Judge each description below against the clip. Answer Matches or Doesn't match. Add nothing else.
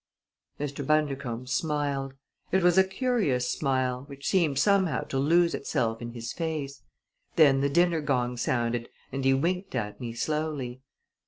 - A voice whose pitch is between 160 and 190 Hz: Doesn't match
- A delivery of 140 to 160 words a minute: Matches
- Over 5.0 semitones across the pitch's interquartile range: Doesn't match